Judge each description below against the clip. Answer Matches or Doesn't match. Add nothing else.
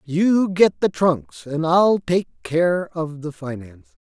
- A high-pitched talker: Doesn't match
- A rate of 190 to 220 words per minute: Doesn't match